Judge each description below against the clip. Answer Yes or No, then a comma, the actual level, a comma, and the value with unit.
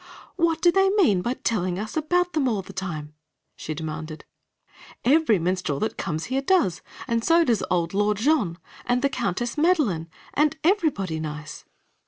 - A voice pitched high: Yes, high, 225 Hz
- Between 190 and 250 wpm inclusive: No, average, 165 wpm